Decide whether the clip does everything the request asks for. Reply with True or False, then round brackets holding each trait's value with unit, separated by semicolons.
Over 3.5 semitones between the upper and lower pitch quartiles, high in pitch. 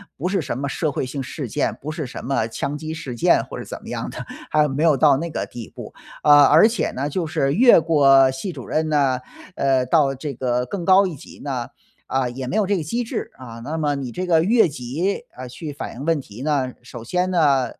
False (3.9 semitones; 145 Hz)